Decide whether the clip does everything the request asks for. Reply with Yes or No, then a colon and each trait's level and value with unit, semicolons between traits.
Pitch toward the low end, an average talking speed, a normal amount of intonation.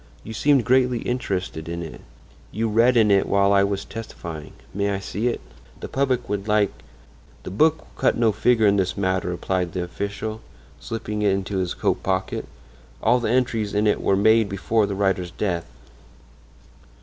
Yes: low, 100 Hz; average, 180 wpm; average, 3.0 semitones